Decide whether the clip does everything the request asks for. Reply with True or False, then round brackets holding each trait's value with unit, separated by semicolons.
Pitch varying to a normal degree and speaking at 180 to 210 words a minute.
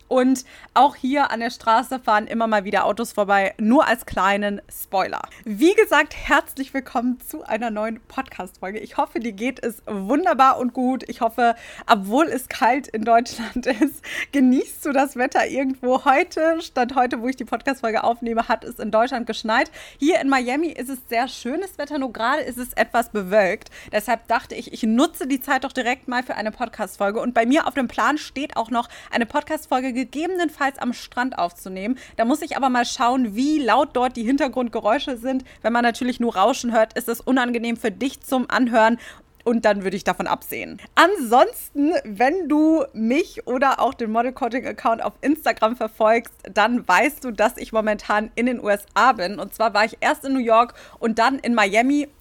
True (3.3 semitones; 190 wpm)